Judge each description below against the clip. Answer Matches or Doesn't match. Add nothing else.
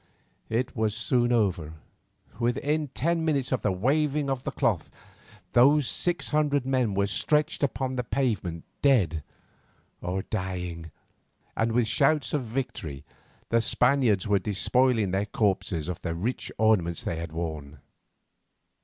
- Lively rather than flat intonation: Matches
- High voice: Doesn't match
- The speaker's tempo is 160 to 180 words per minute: Doesn't match